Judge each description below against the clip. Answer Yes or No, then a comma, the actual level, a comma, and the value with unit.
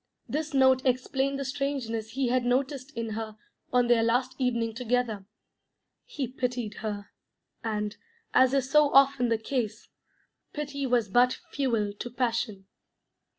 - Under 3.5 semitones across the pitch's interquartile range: Yes, average, 3.0 semitones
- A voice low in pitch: No, high, 245 Hz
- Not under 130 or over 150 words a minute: Yes, average, 140 wpm